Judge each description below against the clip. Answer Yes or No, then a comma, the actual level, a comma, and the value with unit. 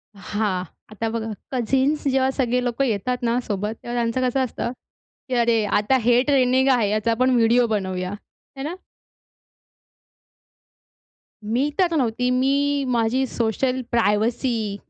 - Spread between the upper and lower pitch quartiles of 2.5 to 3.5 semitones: Yes, average, 2.8 semitones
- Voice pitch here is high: Yes, high, 240 Hz